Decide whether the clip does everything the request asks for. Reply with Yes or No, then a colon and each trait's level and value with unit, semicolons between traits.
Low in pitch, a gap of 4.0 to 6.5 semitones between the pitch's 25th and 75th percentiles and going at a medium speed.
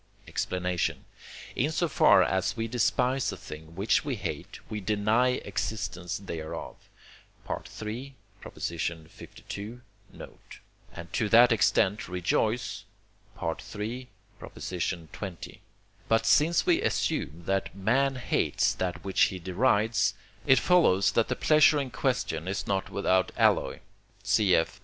No: low, 105 Hz; average, 5.0 semitones; slow, 120 wpm